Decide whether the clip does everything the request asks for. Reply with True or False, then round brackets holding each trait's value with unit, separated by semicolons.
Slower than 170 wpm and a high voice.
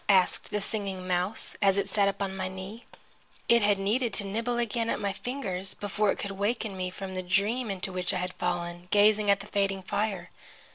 False (205 wpm; 200 Hz)